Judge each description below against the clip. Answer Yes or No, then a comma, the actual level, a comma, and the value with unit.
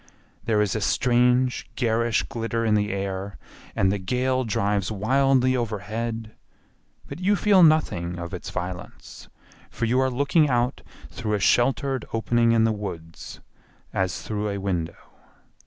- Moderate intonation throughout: Yes, average, 4.1 semitones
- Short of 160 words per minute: Yes, average, 145 wpm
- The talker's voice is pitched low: Yes, low, 115 Hz